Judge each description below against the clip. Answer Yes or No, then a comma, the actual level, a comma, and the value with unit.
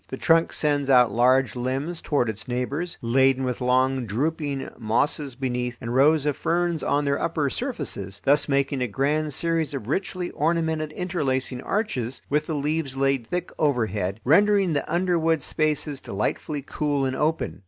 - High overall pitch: No, medium, 140 Hz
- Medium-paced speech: Yes, average, 160 wpm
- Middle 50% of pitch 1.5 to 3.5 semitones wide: No, average, 3.9 semitones